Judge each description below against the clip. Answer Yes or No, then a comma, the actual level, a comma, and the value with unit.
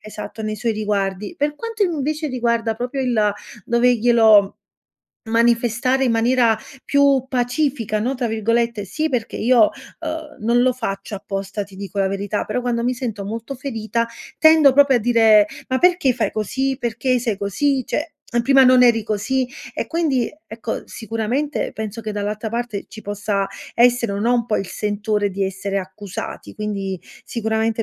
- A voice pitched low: No, high, 230 Hz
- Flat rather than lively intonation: No, average, 3.4 semitones